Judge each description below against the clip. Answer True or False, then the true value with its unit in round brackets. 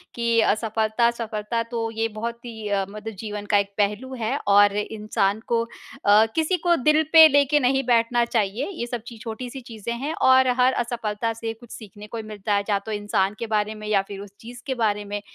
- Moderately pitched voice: False (225 Hz)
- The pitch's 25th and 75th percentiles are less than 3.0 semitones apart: True (2.5 semitones)